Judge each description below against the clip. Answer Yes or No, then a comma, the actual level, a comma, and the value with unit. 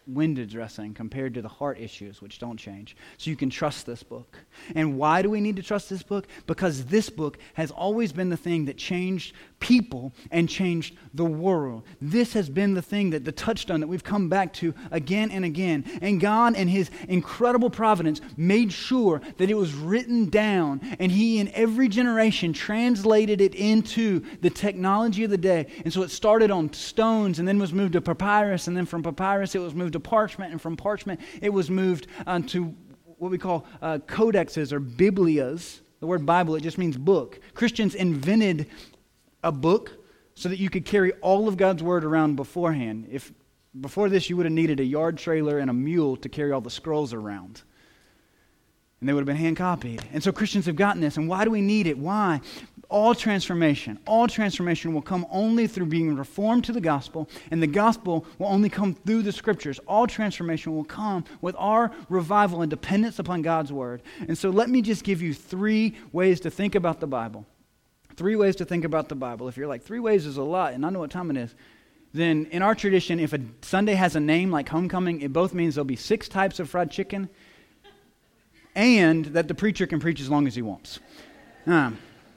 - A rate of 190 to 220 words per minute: Yes, fast, 205 wpm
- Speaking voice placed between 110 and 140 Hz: No, medium, 180 Hz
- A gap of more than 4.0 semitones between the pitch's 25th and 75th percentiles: Yes, average, 4.7 semitones